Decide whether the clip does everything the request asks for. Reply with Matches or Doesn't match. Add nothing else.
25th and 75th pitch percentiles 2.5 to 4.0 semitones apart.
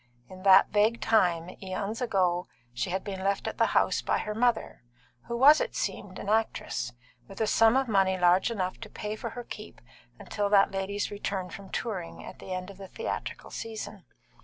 Matches